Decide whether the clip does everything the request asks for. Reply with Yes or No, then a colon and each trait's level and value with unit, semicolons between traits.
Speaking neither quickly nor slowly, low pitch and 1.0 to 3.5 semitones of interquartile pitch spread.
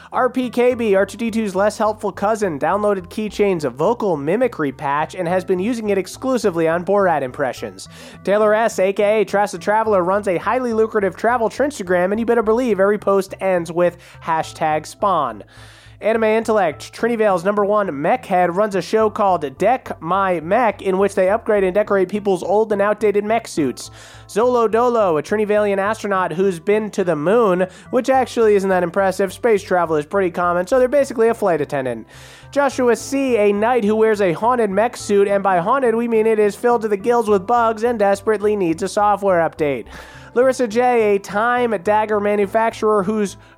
No: average, 180 wpm; high, 205 Hz; average, 3.0 semitones